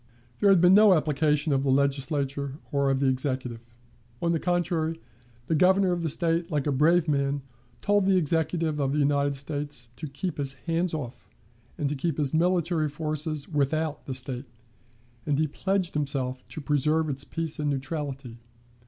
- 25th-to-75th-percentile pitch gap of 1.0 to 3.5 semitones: Yes, average, 3.1 semitones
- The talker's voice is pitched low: No, medium, 150 Hz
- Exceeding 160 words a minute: Yes, average, 175 wpm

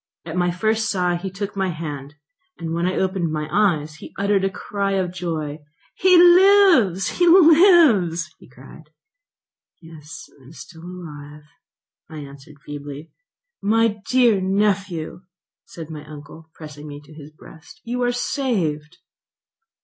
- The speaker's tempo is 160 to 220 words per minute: No, average, 140 wpm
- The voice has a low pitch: No, medium, 175 Hz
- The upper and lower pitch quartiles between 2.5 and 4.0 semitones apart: No, average, 5.3 semitones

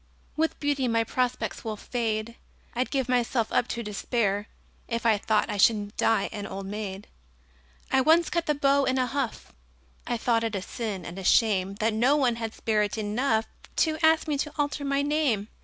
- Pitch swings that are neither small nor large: Yes, average, 4.6 semitones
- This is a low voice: No, high, 230 Hz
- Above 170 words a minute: Yes, average, 190 wpm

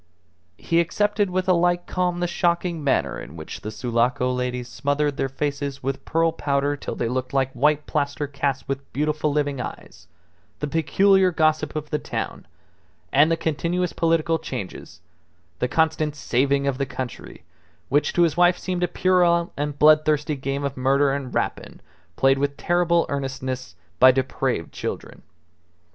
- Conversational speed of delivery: Yes, average, 160 wpm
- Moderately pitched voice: Yes, medium, 145 Hz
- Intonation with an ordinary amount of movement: Yes, average, 3.7 semitones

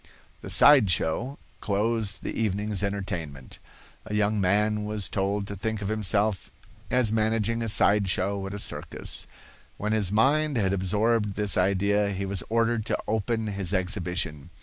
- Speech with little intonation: Yes, narrow, 2.0 semitones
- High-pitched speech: No, low, 105 Hz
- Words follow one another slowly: No, average, 155 wpm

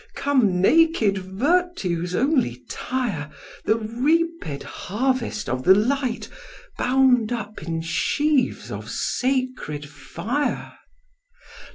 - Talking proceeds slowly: Yes, slow, 90 wpm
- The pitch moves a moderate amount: No, wide, 7.0 semitones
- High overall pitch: Yes, high, 230 Hz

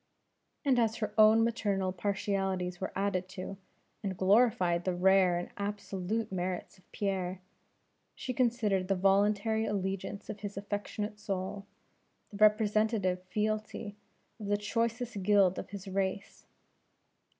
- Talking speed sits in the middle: No, slow, 130 wpm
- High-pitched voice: Yes, high, 200 Hz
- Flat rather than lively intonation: Yes, narrow, 2.2 semitones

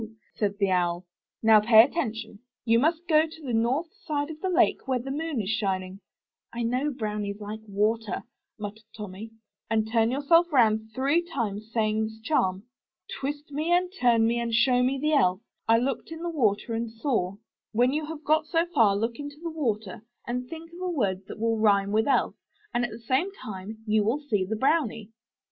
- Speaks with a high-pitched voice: Yes, high, 230 Hz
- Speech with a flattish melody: No, wide, 5.4 semitones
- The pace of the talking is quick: Yes, fast, 210 wpm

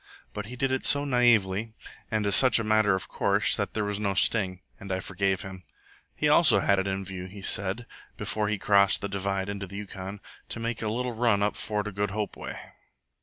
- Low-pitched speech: Yes, low, 100 Hz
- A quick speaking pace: Yes, fast, 220 wpm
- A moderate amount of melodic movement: No, narrow, 2.2 semitones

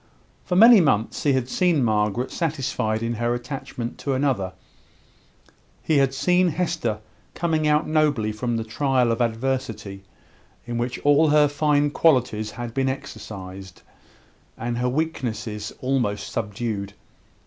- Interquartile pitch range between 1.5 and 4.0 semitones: No, average, 4.9 semitones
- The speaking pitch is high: No, low, 125 Hz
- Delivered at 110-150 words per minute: Yes, slow, 135 wpm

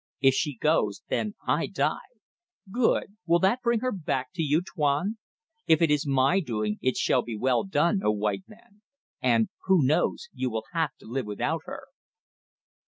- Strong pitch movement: Yes, wide, 7.3 semitones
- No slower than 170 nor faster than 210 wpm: Yes, average, 180 wpm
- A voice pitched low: No, medium, 150 Hz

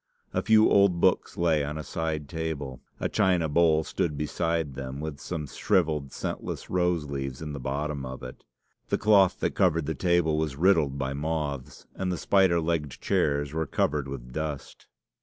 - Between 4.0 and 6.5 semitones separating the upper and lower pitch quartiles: No, average, 3.3 semitones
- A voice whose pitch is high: No, very low, 75 Hz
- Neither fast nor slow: Yes, average, 175 wpm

